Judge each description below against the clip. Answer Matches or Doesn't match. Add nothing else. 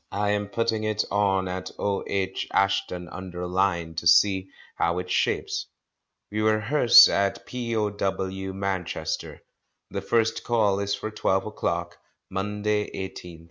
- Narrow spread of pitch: Matches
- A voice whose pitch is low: Matches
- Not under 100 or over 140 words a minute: Matches